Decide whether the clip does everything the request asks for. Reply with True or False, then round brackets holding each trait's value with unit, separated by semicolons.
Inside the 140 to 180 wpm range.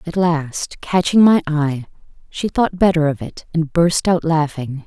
True (175 wpm)